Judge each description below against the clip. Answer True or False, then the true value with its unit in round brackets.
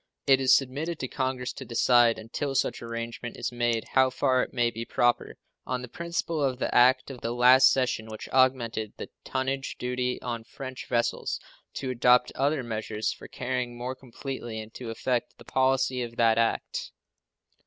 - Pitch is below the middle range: True (125 Hz)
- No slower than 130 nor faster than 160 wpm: False (175 wpm)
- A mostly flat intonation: True (2.0 semitones)